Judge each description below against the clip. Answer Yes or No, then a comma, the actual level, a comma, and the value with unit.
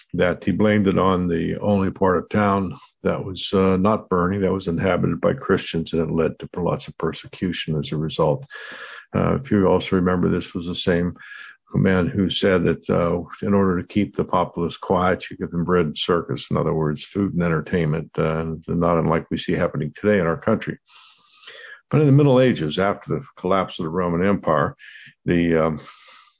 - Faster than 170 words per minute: Yes, average, 195 wpm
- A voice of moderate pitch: No, very low, 90 Hz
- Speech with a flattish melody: No, average, 3.2 semitones